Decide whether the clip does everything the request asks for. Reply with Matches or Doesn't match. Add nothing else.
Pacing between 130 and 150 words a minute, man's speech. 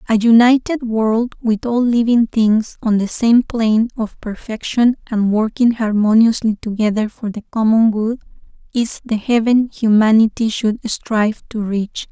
Doesn't match